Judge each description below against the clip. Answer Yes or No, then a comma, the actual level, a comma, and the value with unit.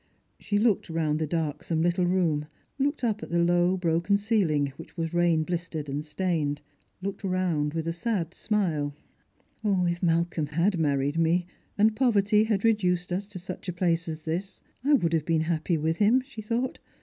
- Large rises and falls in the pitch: No, average, 3.8 semitones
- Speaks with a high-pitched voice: No, medium, 175 Hz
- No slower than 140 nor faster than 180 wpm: No, average, 190 wpm